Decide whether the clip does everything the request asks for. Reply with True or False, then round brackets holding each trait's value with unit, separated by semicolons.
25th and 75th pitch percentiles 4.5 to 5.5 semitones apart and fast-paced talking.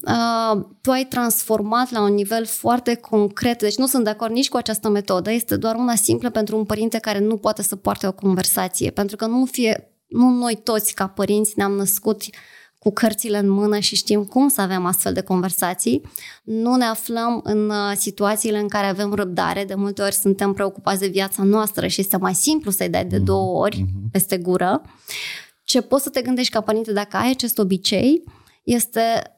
False (2.7 semitones; 190 wpm)